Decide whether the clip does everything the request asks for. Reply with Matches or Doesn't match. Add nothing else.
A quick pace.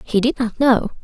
Matches